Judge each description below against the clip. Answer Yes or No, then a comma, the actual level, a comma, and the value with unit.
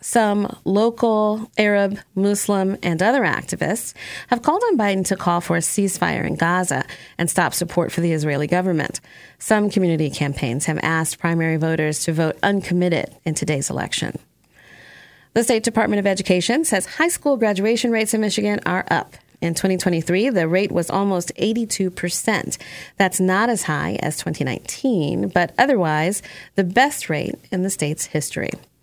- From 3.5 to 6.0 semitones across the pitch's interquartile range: Yes, average, 4.3 semitones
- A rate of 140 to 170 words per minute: Yes, average, 155 wpm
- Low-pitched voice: No, high, 190 Hz